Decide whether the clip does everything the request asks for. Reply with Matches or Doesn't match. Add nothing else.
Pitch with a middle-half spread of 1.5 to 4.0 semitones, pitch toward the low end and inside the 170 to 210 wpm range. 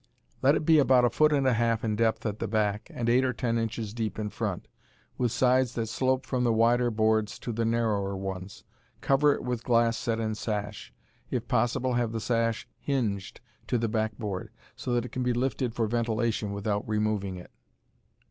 Matches